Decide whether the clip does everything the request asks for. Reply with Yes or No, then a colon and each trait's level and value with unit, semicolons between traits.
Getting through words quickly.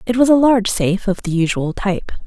Yes: fast, 240 wpm